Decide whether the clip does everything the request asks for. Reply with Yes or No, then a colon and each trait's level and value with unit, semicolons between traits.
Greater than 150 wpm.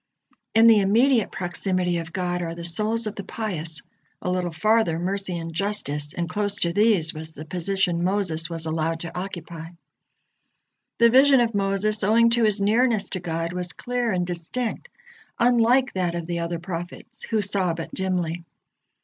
Yes: average, 170 wpm